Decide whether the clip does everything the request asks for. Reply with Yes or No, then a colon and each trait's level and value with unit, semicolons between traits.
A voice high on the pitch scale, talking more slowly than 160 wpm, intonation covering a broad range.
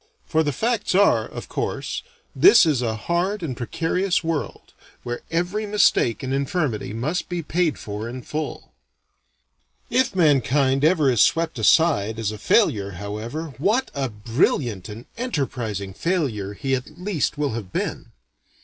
No: medium, 140 Hz; average, 150 wpm; wide, 7.1 semitones